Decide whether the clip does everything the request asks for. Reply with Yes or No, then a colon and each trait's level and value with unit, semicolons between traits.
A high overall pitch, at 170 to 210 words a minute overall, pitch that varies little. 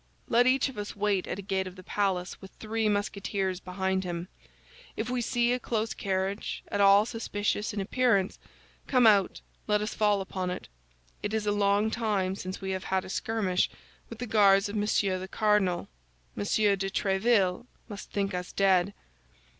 Yes: high, 200 Hz; average, 180 wpm; narrow, 2.2 semitones